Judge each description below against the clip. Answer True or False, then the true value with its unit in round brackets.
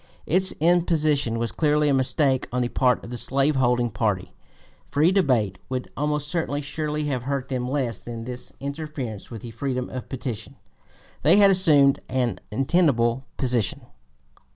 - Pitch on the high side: False (135 Hz)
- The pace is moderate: True (155 wpm)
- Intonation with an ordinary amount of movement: True (3.6 semitones)